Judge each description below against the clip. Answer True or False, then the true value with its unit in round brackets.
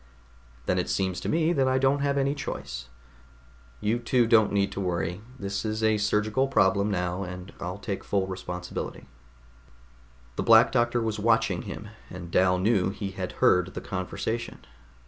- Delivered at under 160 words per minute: False (165 wpm)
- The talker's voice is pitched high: False (100 Hz)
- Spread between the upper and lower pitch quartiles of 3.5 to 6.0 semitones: True (4.1 semitones)